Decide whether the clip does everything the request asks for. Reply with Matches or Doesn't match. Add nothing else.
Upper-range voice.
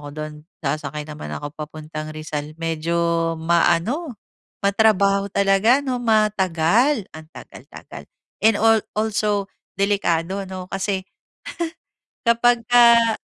Matches